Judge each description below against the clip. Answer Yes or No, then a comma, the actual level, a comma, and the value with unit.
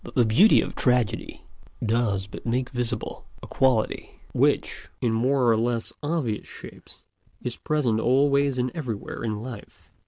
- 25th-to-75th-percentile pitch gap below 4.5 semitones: Yes, average, 2.9 semitones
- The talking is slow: No, average, 150 wpm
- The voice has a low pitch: Yes, low, 120 Hz